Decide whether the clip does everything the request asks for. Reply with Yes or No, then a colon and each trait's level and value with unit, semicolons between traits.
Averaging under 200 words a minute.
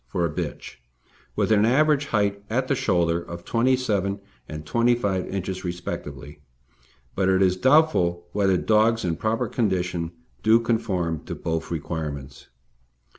Yes: average, 140 wpm